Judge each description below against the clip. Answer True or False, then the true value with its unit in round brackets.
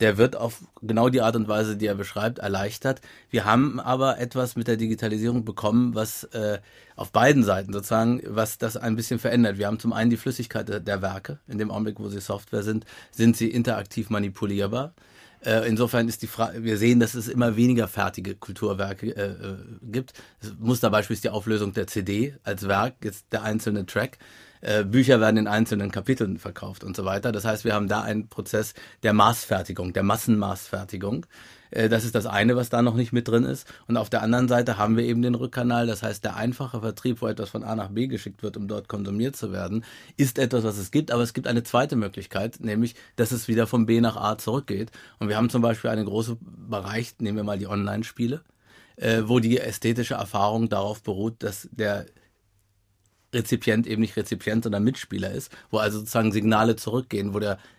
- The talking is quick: True (195 wpm)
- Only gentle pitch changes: True (2.3 semitones)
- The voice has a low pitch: True (110 Hz)